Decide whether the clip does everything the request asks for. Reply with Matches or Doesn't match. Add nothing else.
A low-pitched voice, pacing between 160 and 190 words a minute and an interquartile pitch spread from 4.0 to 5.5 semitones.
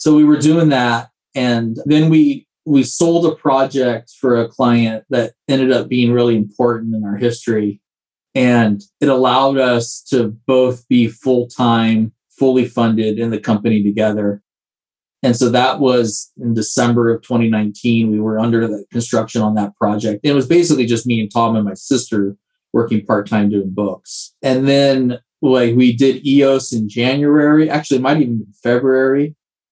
Doesn't match